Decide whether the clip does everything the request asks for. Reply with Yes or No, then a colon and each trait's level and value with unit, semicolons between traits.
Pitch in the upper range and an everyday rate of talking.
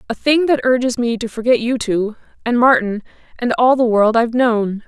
Yes: high, 235 Hz; average, 185 wpm